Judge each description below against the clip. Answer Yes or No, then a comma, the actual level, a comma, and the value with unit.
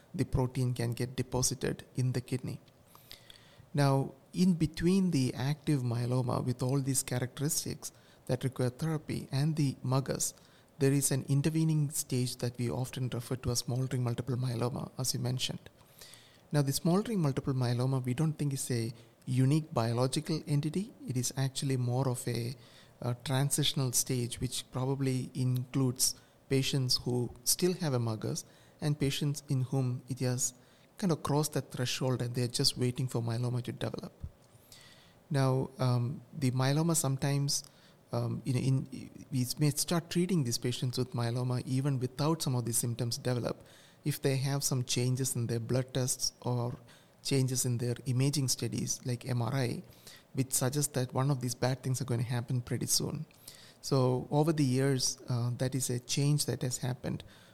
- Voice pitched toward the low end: Yes, low, 130 Hz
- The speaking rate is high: No, average, 165 wpm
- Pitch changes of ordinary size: No, narrow, 2.3 semitones